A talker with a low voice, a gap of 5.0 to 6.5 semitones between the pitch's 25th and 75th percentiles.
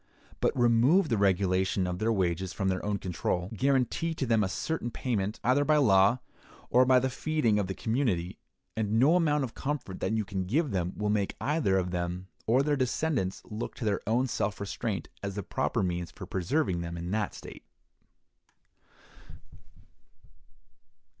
Yes: low, 105 Hz; wide, 5.5 semitones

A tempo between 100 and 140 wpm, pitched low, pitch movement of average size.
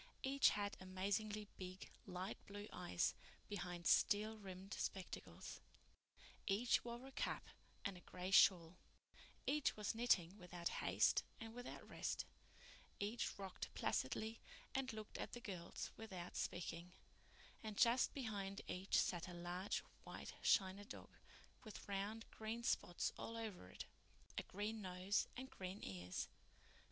No: slow, 135 wpm; high, 200 Hz; average, 3.4 semitones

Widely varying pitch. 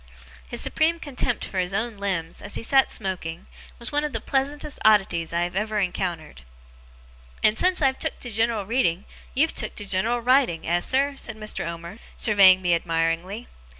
Yes: wide, 6.2 semitones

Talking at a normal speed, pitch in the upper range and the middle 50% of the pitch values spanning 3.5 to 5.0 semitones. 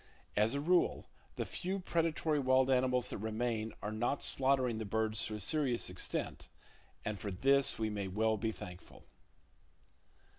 No: average, 155 wpm; low, 115 Hz; average, 4.2 semitones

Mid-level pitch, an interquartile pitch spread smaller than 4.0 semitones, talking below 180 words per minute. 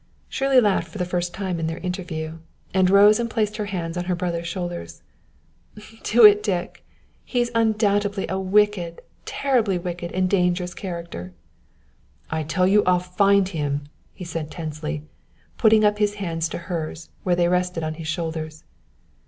Yes: medium, 180 Hz; average, 3.4 semitones; average, 165 wpm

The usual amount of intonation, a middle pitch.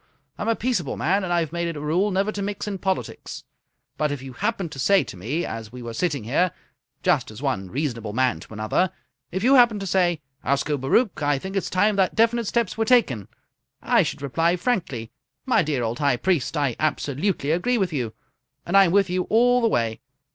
No: wide, 6.8 semitones; medium, 170 Hz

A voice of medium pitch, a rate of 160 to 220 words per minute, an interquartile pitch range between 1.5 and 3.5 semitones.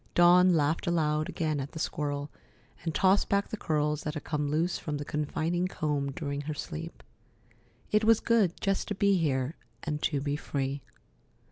Yes: medium, 155 Hz; average, 175 wpm; average, 3.2 semitones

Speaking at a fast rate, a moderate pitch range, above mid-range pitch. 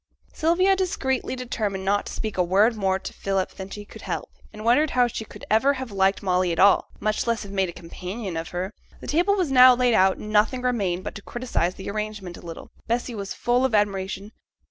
Yes: fast, 225 wpm; average, 4.4 semitones; high, 210 Hz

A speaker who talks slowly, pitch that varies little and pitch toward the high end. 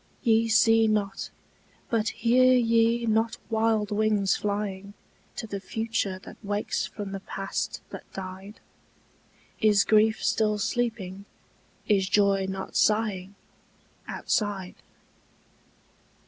Yes: slow, 105 wpm; narrow, 2.2 semitones; high, 210 Hz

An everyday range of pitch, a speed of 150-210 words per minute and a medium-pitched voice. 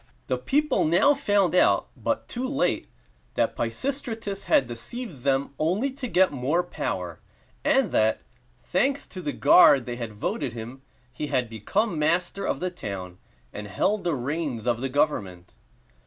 No: wide, 8.8 semitones; average, 155 wpm; medium, 155 Hz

